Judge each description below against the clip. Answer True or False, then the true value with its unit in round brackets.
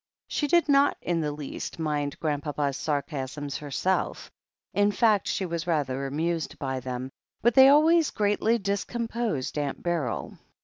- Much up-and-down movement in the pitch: True (7.1 semitones)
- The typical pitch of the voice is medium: True (165 Hz)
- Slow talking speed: False (150 wpm)